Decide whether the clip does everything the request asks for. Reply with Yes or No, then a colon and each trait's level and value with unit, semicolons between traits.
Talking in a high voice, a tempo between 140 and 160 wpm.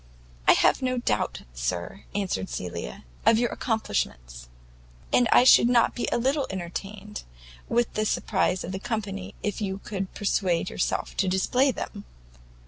Yes: high, 195 Hz; average, 150 wpm